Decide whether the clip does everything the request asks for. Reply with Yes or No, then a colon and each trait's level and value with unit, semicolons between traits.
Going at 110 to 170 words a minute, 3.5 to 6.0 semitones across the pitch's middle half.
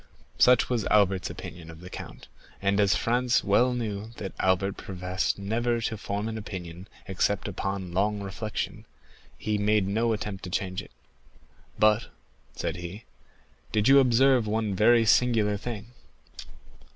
No: average, 145 wpm; average, 2.8 semitones